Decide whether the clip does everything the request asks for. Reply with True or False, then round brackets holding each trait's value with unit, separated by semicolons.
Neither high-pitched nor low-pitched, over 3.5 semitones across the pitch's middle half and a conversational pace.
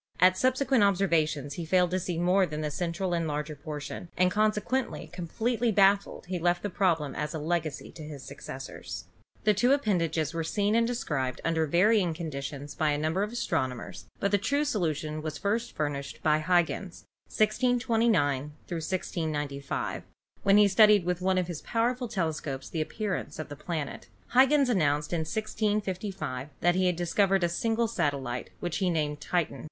True (175 Hz; 5.2 semitones; 170 wpm)